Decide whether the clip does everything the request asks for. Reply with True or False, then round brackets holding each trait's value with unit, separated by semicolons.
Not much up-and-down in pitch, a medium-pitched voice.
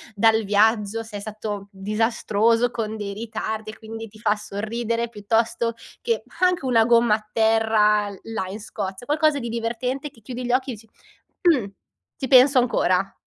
False (2.1 semitones; 225 Hz)